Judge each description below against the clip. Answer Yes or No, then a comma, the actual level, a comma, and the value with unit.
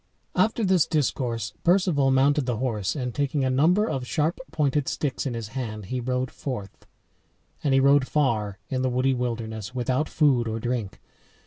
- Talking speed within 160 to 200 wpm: Yes, average, 175 wpm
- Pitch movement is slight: No, average, 3.5 semitones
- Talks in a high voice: No, low, 130 Hz